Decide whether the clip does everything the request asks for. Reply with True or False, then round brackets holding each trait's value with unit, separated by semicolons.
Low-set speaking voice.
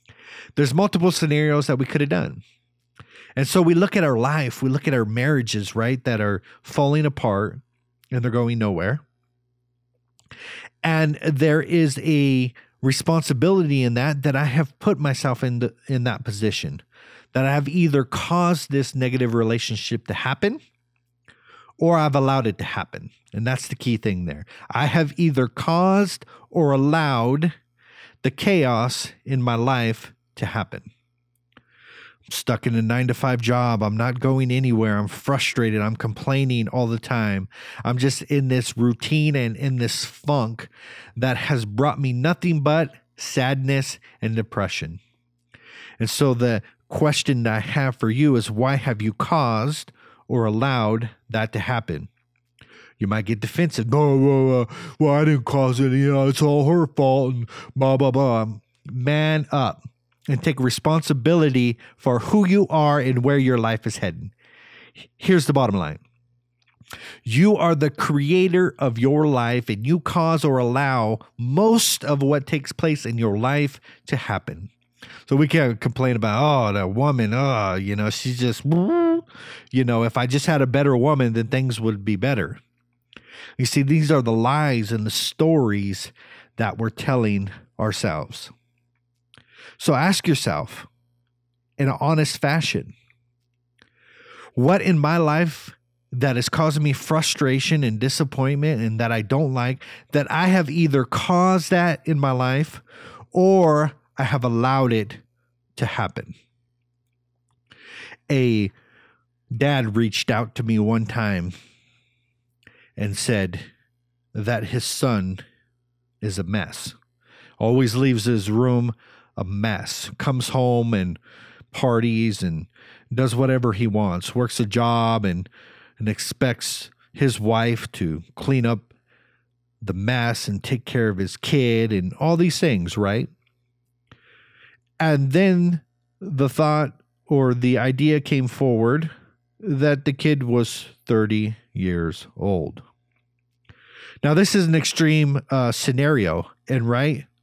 True (125 Hz)